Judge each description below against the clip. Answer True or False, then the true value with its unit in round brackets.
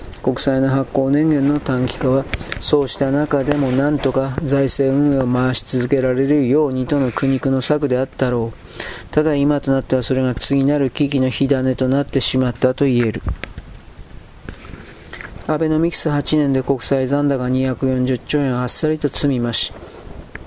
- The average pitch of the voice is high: False (135 Hz)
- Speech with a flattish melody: True (1.8 semitones)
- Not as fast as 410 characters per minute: True (310 characters per minute)